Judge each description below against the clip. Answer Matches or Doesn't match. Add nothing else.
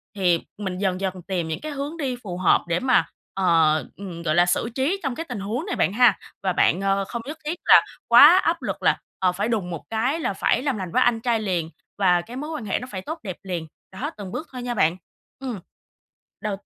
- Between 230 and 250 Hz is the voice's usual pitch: Doesn't match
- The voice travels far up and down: Matches